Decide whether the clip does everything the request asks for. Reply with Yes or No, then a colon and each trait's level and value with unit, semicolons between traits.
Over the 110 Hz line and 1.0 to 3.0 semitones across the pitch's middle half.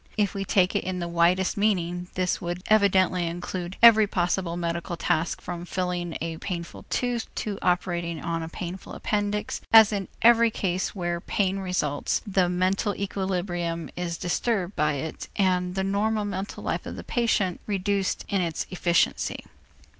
Yes: medium, 185 Hz; narrow, 2.6 semitones